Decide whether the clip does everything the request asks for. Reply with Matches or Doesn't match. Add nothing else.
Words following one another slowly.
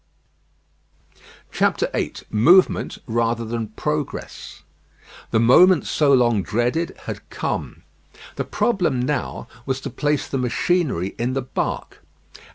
Matches